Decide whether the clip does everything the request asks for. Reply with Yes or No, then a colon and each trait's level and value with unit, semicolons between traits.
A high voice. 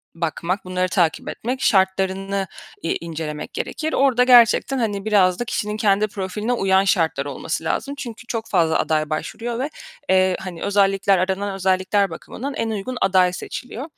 Yes: high, 195 Hz